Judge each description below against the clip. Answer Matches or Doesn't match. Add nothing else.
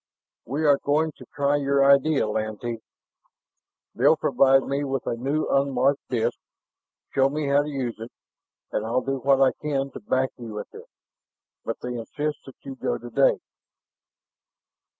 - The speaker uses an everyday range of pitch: Doesn't match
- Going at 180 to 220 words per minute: Doesn't match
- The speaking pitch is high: Doesn't match